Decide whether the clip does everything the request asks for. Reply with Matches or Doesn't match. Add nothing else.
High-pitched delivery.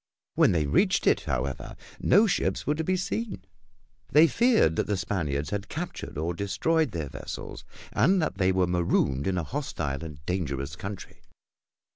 Doesn't match